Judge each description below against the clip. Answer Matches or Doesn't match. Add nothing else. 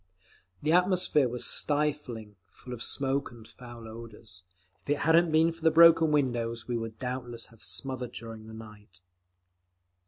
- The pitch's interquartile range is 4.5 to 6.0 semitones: Matches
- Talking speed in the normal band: Matches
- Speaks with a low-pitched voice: Matches